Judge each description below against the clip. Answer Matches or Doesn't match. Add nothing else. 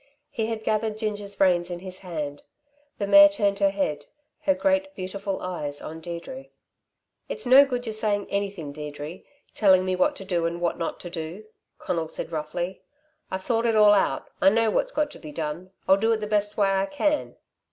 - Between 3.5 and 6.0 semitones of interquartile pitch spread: Matches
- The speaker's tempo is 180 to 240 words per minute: Matches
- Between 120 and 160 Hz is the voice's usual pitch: Doesn't match